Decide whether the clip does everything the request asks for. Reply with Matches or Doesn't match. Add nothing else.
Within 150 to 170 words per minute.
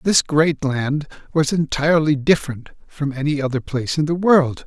Matches